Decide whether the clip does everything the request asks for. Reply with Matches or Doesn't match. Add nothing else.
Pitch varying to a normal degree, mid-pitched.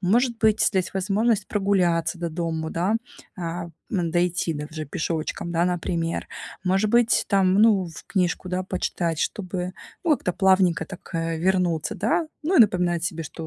Matches